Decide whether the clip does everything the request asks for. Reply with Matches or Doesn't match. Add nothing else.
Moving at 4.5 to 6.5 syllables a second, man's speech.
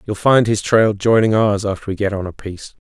Matches